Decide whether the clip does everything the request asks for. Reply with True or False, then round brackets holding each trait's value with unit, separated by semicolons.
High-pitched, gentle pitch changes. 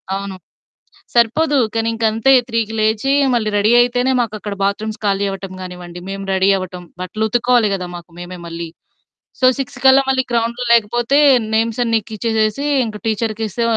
False (220 Hz; 3.2 semitones)